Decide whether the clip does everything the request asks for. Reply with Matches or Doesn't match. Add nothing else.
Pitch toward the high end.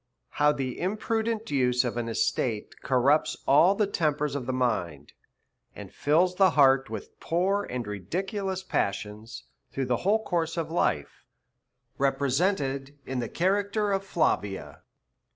Doesn't match